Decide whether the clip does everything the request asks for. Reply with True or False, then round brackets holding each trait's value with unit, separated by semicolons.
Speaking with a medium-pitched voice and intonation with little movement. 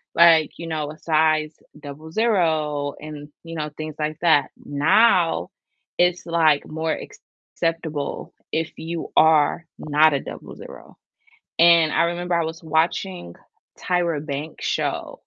True (160 Hz; 1.8 semitones)